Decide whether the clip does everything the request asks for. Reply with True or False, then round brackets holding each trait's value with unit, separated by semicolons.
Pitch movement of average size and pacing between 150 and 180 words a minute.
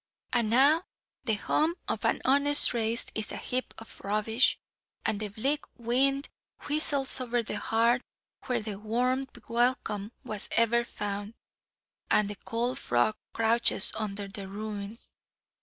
False (3.2 semitones; 140 wpm)